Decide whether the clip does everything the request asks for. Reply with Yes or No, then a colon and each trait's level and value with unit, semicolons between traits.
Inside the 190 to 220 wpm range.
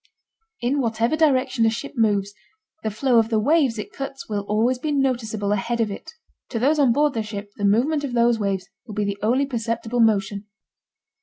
Yes: average, 200 wpm